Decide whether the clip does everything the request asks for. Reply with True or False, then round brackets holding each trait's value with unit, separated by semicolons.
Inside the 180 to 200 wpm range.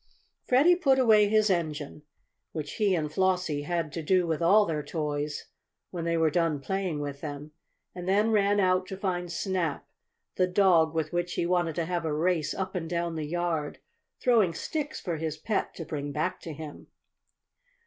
True (185 wpm)